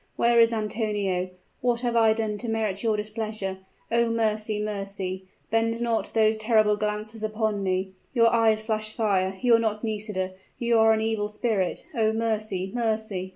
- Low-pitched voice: No, high, 215 Hz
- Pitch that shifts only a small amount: Yes, narrow, 1.5 semitones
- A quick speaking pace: No, average, 165 wpm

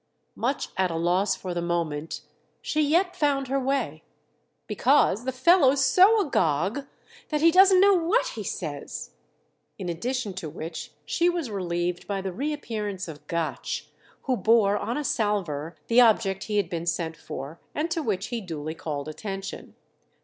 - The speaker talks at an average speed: Yes, average, 165 wpm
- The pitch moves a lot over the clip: Yes, wide, 8.3 semitones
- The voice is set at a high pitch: Yes, high, 210 Hz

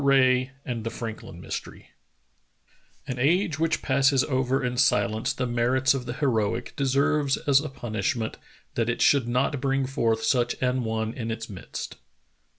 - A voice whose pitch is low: Yes, low, 130 Hz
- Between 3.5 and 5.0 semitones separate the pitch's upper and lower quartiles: No, average, 2.7 semitones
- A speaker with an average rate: Yes, average, 155 wpm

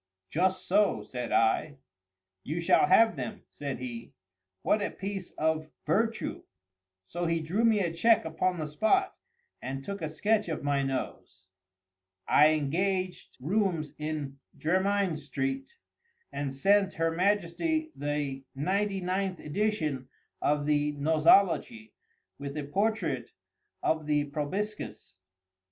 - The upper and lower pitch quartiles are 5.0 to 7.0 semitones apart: Yes, average, 5.3 semitones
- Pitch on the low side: No, medium, 165 Hz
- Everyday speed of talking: No, slow, 125 wpm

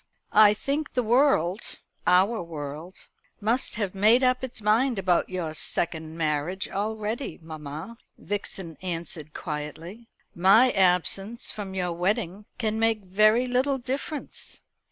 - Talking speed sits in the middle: No, slow, 125 wpm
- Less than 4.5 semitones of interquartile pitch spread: No, average, 5.3 semitones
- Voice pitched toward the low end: No, high, 195 Hz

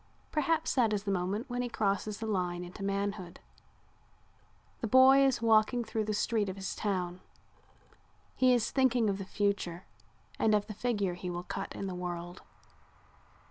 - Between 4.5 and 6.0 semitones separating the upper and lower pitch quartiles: No, average, 3.9 semitones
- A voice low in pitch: No, high, 205 Hz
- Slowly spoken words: No, average, 170 wpm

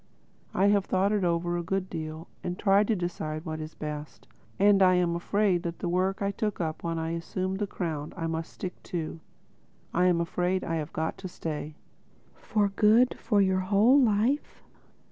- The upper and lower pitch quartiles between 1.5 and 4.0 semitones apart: Yes, average, 3.3 semitones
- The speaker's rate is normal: Yes, average, 175 wpm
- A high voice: No, medium, 180 Hz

